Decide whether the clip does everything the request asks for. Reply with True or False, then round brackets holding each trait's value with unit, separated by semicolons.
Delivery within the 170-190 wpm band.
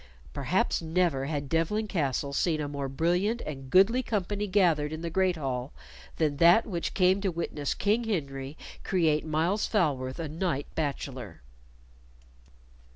False (145 wpm)